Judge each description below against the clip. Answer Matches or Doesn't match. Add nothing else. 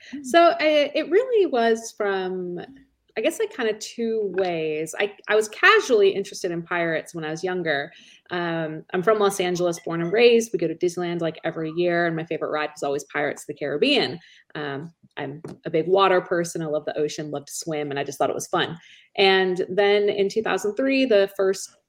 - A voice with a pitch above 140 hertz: Matches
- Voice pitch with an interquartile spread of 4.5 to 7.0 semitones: Matches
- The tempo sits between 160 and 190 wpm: Doesn't match